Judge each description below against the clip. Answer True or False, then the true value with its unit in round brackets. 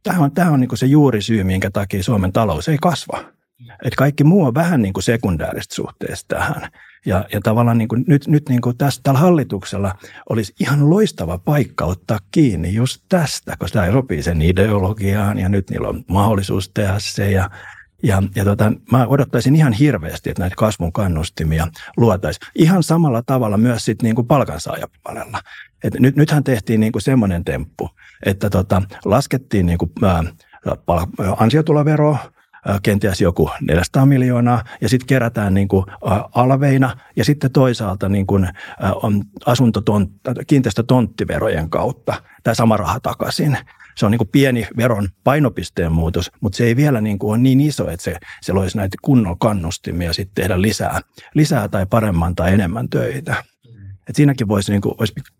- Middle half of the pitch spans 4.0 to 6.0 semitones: True (5.1 semitones)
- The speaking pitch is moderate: False (110 Hz)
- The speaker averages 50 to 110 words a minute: False (155 wpm)